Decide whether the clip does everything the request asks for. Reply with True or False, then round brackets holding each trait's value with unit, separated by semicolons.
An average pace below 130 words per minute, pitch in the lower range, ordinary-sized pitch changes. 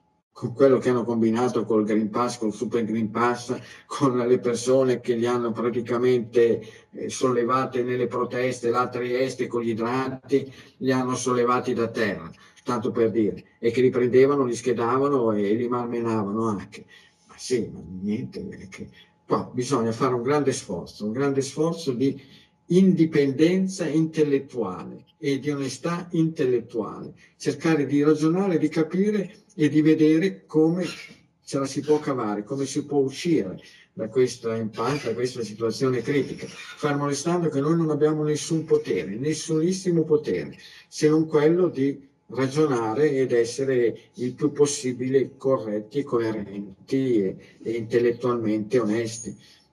False (145 wpm; 130 Hz; 4.1 semitones)